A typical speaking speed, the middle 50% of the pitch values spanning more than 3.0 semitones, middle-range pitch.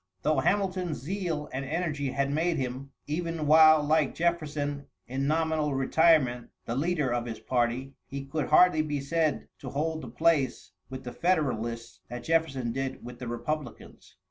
Yes: average, 160 wpm; average, 3.5 semitones; medium, 145 Hz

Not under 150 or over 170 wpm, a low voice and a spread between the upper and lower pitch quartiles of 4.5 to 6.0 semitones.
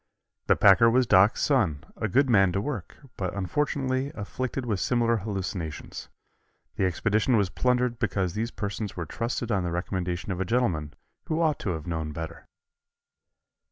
Yes: average, 160 wpm; low, 105 Hz; average, 5.3 semitones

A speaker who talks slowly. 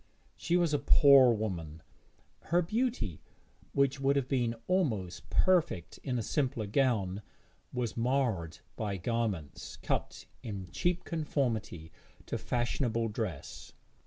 Yes: slow, 120 wpm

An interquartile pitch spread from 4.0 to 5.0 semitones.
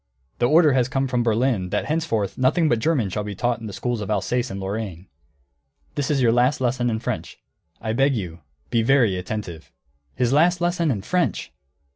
Yes: average, 4.5 semitones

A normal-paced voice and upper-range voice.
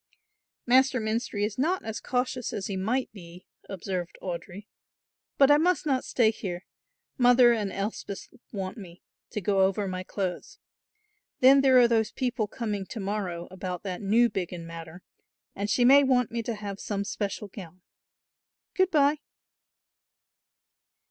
Yes: average, 150 wpm; high, 210 Hz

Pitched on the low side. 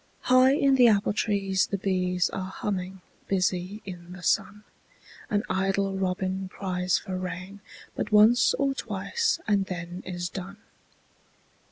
No: high, 190 Hz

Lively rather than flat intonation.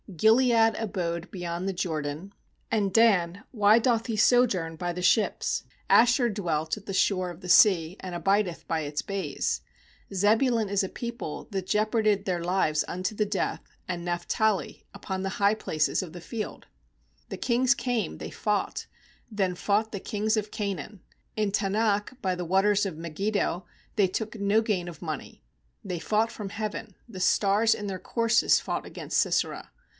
No: average, 3.4 semitones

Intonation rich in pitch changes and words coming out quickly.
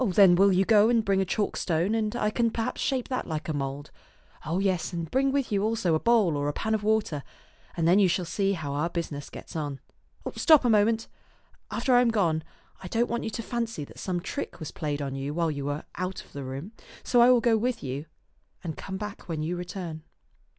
Yes: wide, 6.0 semitones; fast, 240 wpm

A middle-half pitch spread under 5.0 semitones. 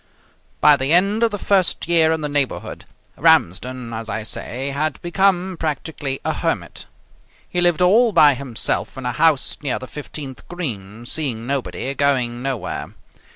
No: average, 5.3 semitones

